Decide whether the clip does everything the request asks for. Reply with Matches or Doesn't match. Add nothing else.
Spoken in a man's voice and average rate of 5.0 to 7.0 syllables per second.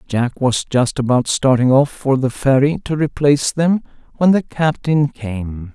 Doesn't match